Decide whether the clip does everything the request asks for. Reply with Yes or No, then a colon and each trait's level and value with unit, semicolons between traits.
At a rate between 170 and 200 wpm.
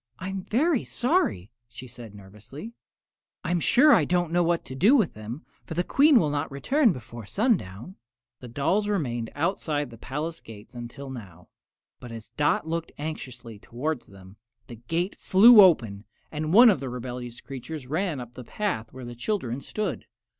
Yes: average, 175 wpm